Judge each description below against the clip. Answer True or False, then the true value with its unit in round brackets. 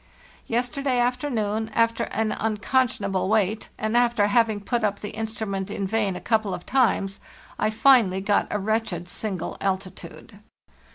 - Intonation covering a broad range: False (2.6 semitones)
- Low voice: False (215 Hz)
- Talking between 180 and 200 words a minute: False (150 wpm)